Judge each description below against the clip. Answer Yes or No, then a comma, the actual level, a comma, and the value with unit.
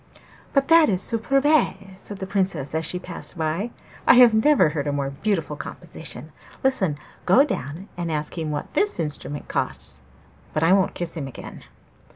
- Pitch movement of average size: No, wide, 6.2 semitones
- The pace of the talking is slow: No, average, 175 wpm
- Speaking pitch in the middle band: Yes, medium, 180 Hz